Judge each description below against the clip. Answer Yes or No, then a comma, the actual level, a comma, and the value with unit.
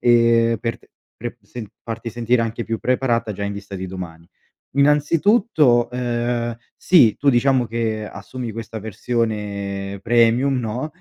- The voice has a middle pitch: No, low, 115 Hz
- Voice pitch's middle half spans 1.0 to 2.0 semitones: No, narrow, 2.5 semitones